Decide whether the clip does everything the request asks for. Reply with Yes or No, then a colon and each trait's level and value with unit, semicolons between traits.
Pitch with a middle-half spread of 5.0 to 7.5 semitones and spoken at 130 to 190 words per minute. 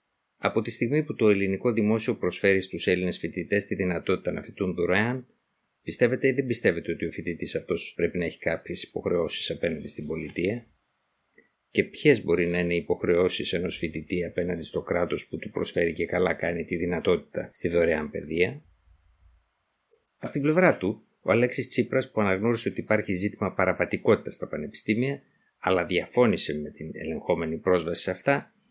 Yes: wide, 5.6 semitones; average, 165 wpm